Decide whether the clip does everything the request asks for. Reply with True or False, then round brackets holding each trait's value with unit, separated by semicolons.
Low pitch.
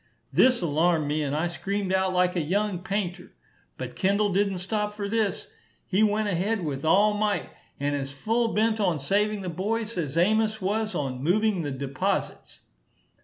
False (190 Hz)